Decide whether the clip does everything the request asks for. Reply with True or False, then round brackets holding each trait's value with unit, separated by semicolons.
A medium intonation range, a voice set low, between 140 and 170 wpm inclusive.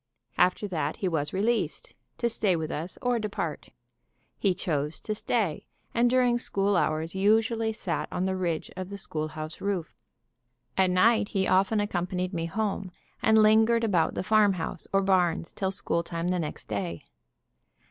False (4.2 semitones; 190 Hz; 160 wpm)